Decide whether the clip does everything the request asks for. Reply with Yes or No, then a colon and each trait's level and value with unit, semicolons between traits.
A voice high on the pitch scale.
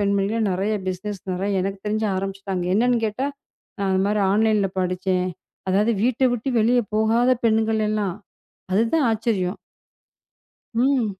Yes: high, 210 Hz